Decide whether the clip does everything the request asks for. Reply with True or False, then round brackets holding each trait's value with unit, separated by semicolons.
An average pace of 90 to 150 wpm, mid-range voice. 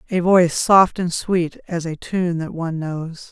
False (200 wpm; 170 Hz)